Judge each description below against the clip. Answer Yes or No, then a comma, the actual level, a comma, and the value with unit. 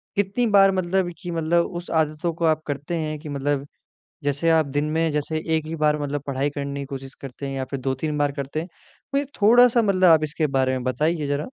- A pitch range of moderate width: Yes, average, 3.2 semitones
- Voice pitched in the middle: Yes, medium, 155 Hz